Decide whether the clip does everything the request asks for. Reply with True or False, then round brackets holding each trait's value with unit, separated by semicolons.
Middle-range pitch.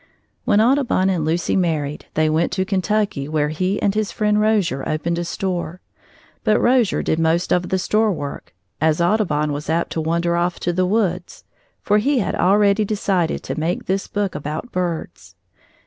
True (180 Hz)